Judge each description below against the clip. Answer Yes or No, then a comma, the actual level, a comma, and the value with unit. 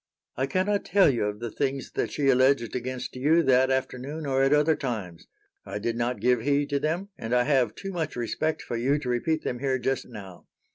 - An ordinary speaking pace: No, fast, 220 wpm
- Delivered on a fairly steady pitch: No, average, 3.3 semitones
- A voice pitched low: Yes, low, 130 Hz